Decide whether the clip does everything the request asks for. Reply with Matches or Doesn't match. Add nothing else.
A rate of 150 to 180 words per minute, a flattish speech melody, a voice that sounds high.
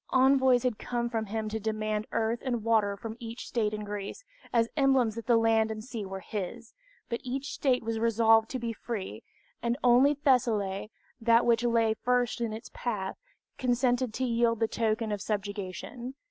Matches